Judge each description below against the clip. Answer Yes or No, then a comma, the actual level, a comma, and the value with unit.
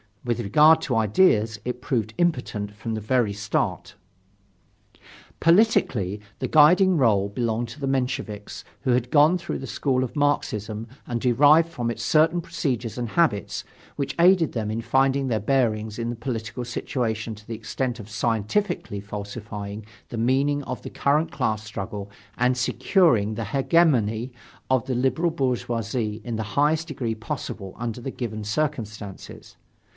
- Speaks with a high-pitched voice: No, low, 120 Hz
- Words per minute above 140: Yes, average, 150 wpm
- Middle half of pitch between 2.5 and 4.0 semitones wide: No, average, 4.4 semitones